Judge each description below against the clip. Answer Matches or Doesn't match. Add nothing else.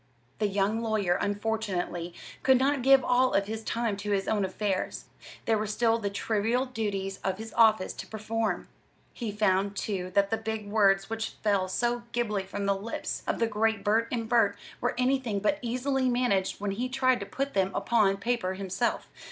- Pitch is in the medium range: Doesn't match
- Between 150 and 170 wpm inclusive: Doesn't match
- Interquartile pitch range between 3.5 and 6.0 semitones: Doesn't match